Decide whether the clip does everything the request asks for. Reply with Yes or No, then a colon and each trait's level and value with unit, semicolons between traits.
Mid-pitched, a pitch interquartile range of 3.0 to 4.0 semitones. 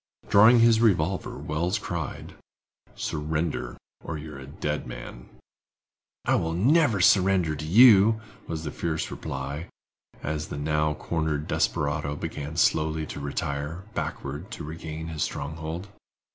No: very low, 80 Hz; average, 3.3 semitones